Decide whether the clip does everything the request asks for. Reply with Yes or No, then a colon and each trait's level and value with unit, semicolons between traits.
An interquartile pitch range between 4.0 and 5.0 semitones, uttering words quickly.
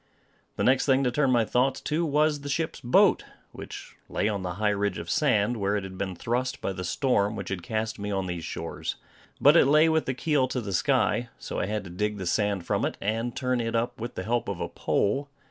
Yes: average, 4.7 semitones; fast, 245 wpm